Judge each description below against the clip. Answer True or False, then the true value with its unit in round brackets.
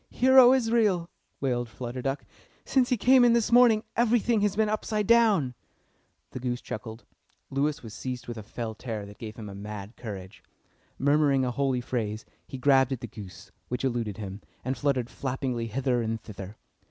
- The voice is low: True (130 Hz)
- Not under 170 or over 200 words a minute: True (180 wpm)